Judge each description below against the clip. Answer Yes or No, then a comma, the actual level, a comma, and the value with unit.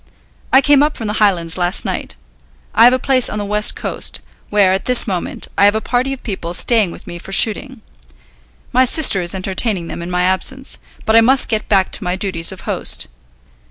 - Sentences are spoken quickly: Yes, fast, 215 wpm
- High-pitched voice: Yes, high, 205 Hz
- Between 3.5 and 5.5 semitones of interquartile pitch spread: Yes, average, 4.8 semitones